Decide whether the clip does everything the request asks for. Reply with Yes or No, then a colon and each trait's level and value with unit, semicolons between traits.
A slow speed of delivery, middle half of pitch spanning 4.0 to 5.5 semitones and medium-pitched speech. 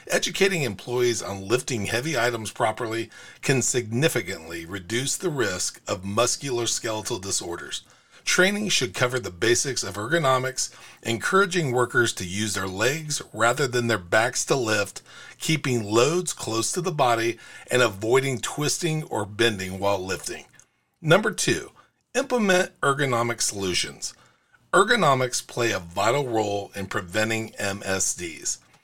No: slow, 125 wpm; average, 4.5 semitones; low, 120 Hz